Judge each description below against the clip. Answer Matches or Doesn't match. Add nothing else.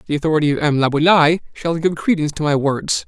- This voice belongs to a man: Matches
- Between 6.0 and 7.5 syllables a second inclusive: Matches